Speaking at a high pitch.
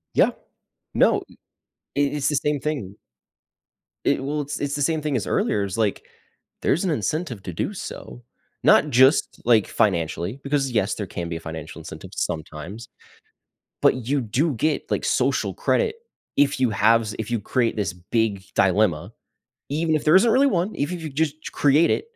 No: low, 130 Hz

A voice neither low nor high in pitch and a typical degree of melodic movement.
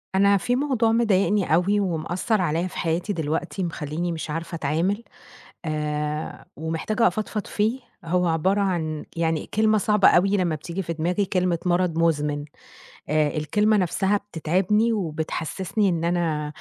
Yes: medium, 175 Hz; average, 4.1 semitones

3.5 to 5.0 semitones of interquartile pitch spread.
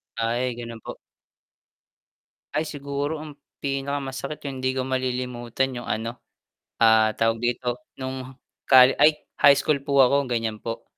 No: average, 2.7 semitones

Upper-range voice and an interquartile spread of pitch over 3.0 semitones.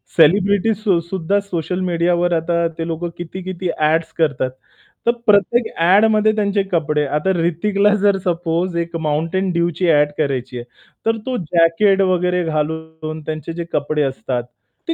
No: medium, 170 Hz; average, 3.4 semitones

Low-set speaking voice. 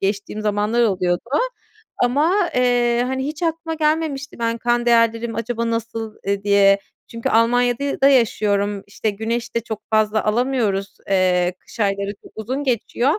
No: high, 230 Hz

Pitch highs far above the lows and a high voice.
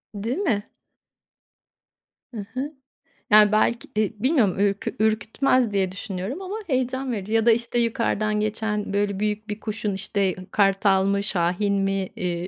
No: average, 2.8 semitones; high, 210 Hz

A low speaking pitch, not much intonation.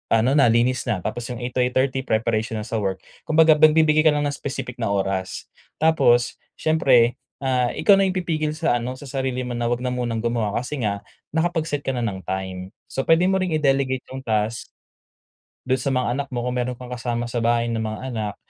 No: low, 125 Hz; average, 3.3 semitones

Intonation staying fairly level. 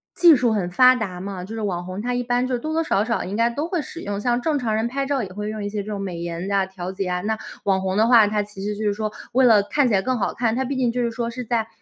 No: average, 3.8 semitones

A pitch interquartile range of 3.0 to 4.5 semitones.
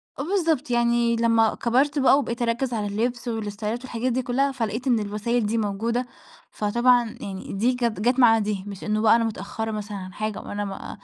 No: narrow, 2.6 semitones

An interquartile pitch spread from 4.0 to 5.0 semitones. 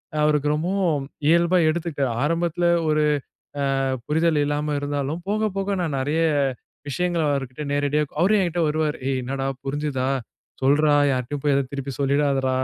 No: average, 3.2 semitones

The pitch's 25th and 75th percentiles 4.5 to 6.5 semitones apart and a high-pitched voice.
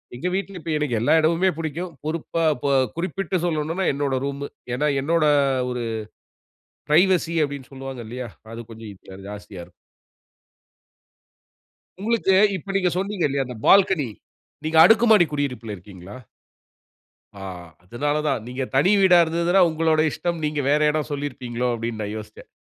No: wide, 5.6 semitones; medium, 150 Hz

